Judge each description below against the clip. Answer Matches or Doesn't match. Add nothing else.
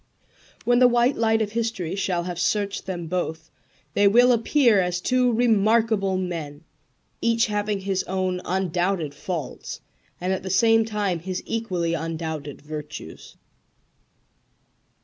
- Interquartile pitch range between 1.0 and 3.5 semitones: Doesn't match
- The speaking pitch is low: Doesn't match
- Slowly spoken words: Matches